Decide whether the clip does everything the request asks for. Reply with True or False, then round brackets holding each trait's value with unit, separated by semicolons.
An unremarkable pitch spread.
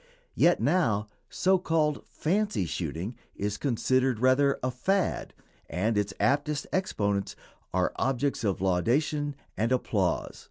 False (6.7 semitones)